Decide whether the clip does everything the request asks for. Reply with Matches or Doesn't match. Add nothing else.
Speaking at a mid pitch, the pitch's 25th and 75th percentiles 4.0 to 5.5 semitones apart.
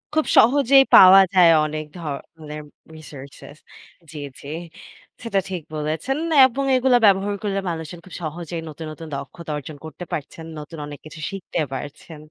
Matches